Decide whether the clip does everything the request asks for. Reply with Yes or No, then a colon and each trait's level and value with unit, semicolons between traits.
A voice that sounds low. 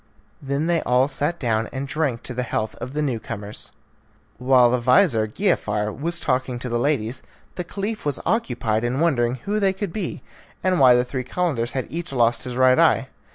Yes: low, 130 Hz